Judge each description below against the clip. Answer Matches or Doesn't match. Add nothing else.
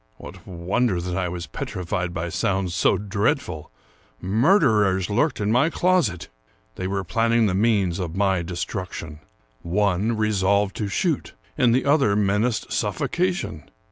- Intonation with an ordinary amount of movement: Matches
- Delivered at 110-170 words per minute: Matches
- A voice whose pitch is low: Matches